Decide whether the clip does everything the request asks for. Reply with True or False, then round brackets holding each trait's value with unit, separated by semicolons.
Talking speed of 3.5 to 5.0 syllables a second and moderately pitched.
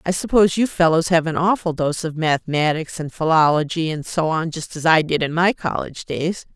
False (5.5 syllables/s; 165 Hz)